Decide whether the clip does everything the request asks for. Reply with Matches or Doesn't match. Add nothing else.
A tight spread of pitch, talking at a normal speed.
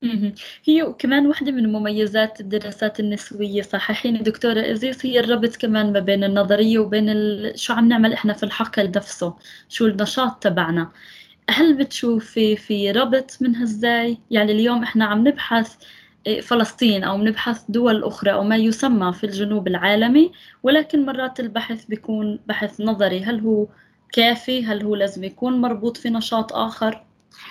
Matches